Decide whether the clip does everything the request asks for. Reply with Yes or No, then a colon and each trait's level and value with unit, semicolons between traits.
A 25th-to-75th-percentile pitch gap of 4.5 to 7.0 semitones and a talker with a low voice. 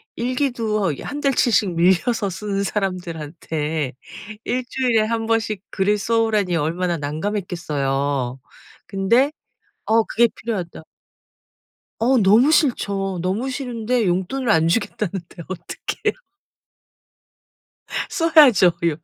No: average, 5.1 semitones; high, 200 Hz